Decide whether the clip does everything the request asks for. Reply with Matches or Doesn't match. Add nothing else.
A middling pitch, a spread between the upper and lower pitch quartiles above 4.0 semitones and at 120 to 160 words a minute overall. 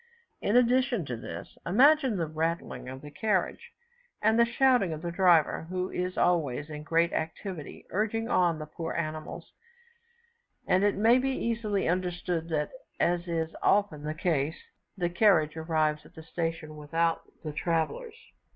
Matches